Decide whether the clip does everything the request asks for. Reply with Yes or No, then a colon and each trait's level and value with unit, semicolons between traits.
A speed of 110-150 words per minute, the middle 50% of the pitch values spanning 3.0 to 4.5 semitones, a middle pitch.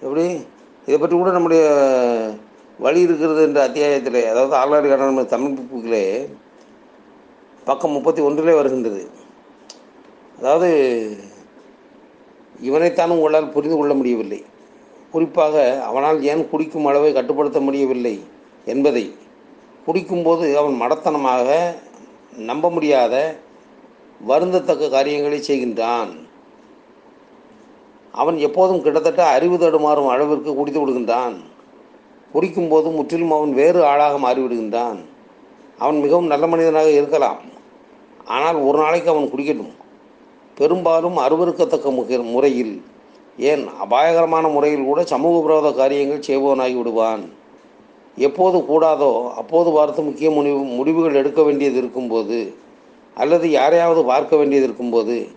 No: average, 100 wpm; average, 3.9 semitones; medium, 145 Hz